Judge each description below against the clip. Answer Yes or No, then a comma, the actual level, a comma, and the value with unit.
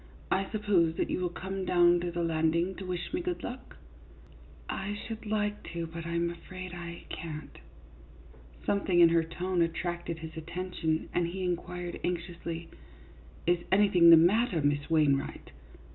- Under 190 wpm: Yes, average, 175 wpm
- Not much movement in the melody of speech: Yes, narrow, 2.1 semitones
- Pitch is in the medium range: Yes, medium, 175 Hz